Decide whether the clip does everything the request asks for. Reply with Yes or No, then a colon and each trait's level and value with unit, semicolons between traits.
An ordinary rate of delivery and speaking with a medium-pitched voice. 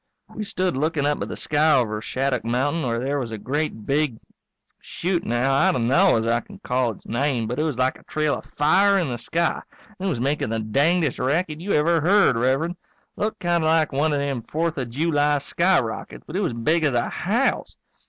No: fast, 220 wpm; medium, 145 Hz